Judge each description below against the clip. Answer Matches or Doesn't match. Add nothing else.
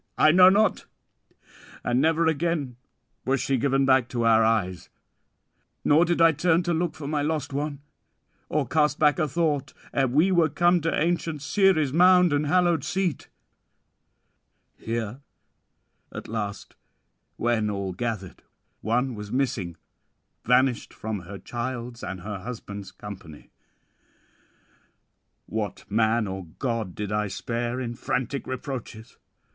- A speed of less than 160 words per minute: Matches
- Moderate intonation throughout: Doesn't match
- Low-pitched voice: Matches